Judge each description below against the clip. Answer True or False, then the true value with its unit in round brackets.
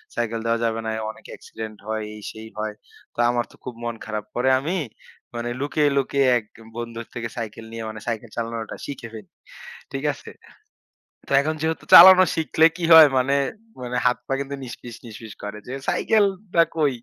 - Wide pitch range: False (4.2 semitones)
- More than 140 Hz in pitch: False (120 Hz)